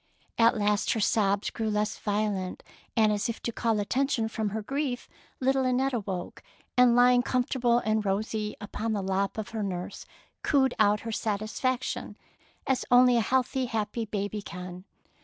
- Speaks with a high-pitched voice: Yes, high, 220 Hz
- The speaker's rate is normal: Yes, average, 160 wpm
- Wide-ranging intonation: No, average, 3.1 semitones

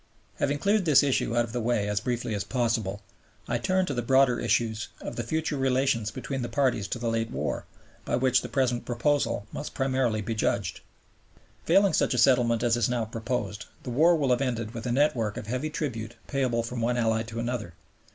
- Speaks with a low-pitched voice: Yes, low, 120 Hz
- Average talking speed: No, fast, 210 wpm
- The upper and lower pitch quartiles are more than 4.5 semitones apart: No, average, 2.7 semitones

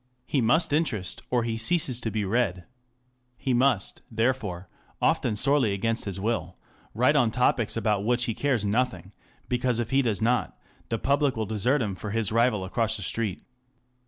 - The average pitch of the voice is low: Yes, low, 115 Hz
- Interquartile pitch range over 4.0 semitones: No, average, 3.1 semitones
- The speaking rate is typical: Yes, average, 175 wpm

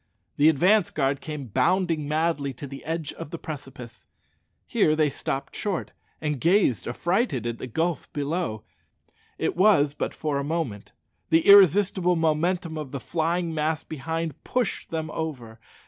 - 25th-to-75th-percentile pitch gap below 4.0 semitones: Yes, average, 3.5 semitones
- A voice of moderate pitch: Yes, medium, 155 Hz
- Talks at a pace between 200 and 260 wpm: No, average, 150 wpm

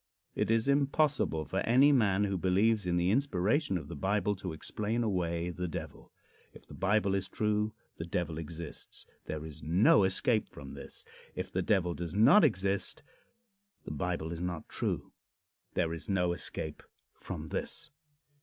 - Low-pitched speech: Yes, very low, 95 Hz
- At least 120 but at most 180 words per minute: Yes, average, 165 wpm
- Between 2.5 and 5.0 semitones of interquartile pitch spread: Yes, average, 4.0 semitones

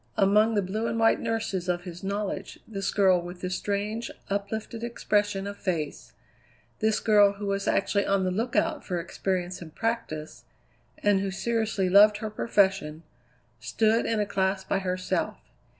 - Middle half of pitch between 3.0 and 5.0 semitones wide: No, narrow, 2.6 semitones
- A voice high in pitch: Yes, high, 200 Hz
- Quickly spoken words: No, average, 160 wpm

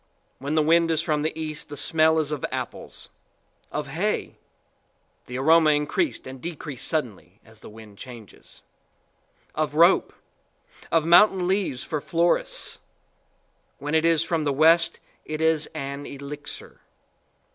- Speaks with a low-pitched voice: No, medium, 155 Hz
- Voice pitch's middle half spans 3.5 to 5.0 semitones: No, average, 2.8 semitones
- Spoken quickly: No, average, 140 wpm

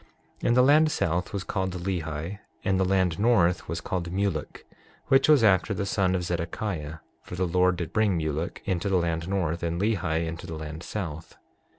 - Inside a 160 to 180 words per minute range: No, average, 195 wpm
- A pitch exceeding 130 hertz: No, very low, 90 Hz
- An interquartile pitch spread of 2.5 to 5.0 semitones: Yes, average, 3.0 semitones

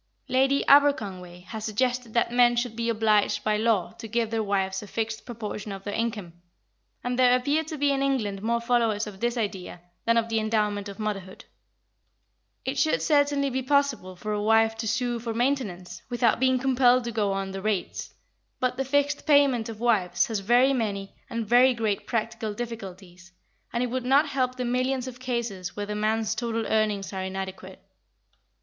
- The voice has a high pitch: Yes, high, 230 Hz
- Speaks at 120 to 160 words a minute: No, average, 185 wpm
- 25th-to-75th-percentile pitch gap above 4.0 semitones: No, average, 3.4 semitones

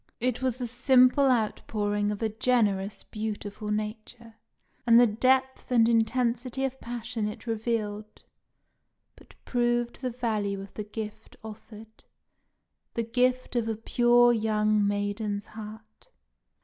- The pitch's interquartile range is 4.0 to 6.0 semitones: No, narrow, 2.4 semitones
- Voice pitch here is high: Yes, high, 225 Hz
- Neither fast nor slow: No, slow, 125 wpm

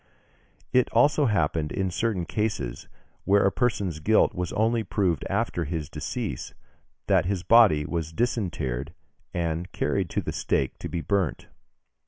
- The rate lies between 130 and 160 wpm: Yes, average, 145 wpm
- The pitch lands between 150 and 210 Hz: No, very low, 90 Hz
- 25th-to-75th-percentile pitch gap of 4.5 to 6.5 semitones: Yes, average, 5.2 semitones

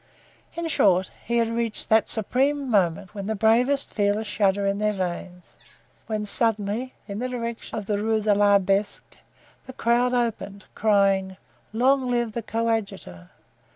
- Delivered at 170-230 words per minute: No, average, 155 wpm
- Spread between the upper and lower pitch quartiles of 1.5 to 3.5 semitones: Yes, average, 2.8 semitones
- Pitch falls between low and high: No, high, 215 Hz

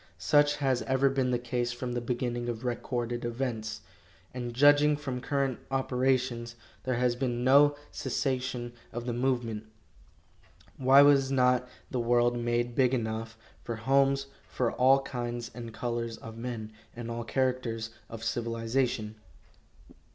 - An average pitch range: No, narrow, 2.0 semitones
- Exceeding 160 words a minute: No, average, 140 wpm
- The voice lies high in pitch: No, low, 120 Hz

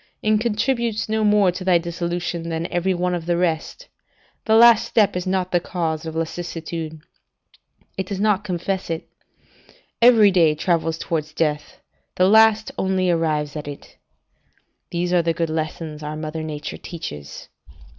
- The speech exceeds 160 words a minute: No, average, 155 wpm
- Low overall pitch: No, medium, 175 Hz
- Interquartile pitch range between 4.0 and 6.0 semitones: No, average, 3.2 semitones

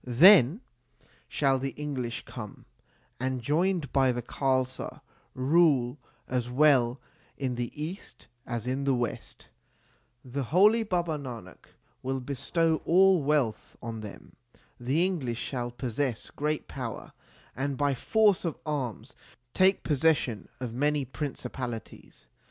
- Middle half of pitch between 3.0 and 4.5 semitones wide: Yes, average, 3.9 semitones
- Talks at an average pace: No, slow, 125 wpm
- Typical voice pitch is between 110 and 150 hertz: Yes, low, 135 Hz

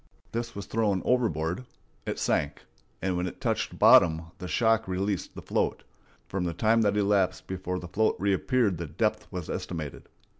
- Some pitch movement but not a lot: Yes, average, 3.7 semitones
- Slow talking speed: No, average, 165 wpm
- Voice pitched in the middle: No, very low, 95 Hz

